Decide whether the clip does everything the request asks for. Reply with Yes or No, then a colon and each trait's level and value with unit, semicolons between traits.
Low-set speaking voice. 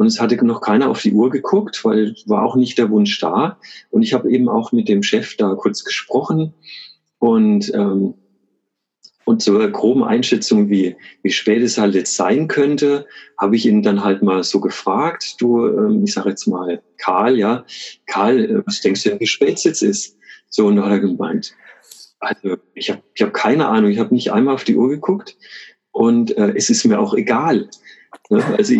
Yes: low, 125 Hz